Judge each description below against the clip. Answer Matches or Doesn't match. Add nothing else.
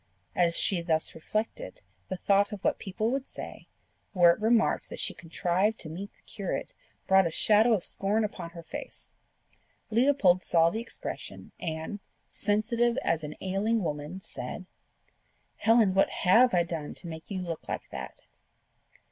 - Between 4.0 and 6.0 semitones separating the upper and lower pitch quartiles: Matches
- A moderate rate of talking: Matches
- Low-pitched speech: Doesn't match